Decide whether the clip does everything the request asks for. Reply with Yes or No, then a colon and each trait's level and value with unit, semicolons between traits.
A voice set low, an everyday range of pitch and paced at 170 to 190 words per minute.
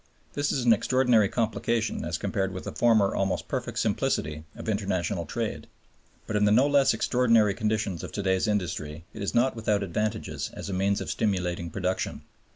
Yes: low, 105 Hz; average, 3.3 semitones; average, 180 wpm